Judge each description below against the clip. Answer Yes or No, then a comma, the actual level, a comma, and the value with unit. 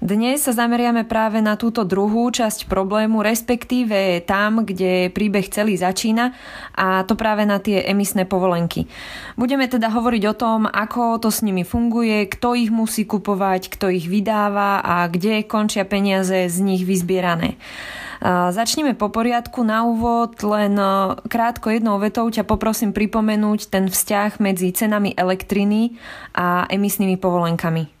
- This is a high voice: Yes, high, 210 Hz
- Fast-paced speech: No, average, 140 wpm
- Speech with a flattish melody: No, average, 3.0 semitones